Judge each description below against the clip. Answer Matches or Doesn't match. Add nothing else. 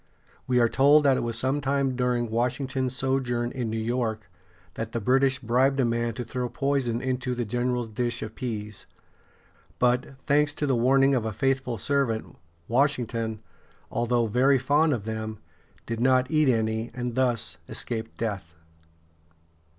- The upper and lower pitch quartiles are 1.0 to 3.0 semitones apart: Matches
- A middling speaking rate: Matches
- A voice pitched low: Matches